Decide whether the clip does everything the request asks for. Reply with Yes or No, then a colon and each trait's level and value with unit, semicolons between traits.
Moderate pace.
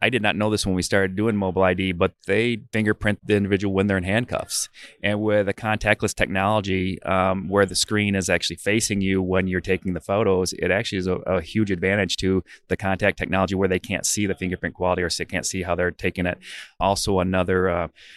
No: fast, 225 wpm